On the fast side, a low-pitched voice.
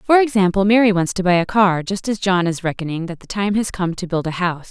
No: fast, 280 wpm; high, 190 Hz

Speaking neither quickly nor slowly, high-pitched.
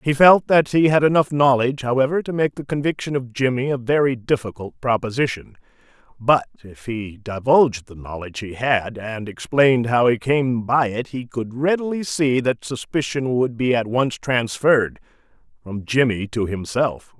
No: average, 170 wpm; low, 125 Hz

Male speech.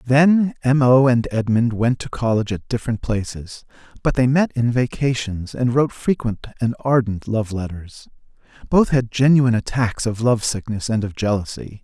Yes: male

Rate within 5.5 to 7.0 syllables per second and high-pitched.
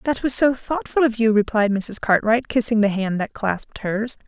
No: 4.9 syllables/s; high, 225 Hz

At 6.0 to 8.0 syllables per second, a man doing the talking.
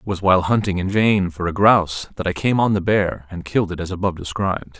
Yes: 6.3 syllables/s; male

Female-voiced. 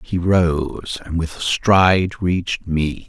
No: male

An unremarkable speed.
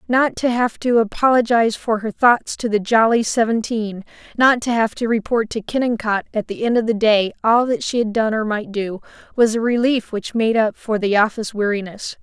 No: fast, 210 wpm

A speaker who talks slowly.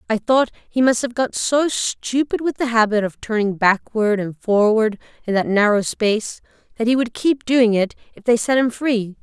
No: average, 200 wpm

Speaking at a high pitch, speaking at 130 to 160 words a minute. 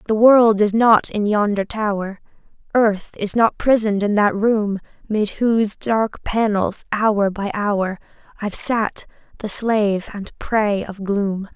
Yes: high, 210 Hz; average, 150 wpm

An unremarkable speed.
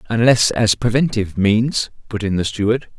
Yes: average, 160 wpm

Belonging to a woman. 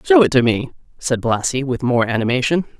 Yes: female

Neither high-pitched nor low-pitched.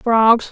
No: high, 225 Hz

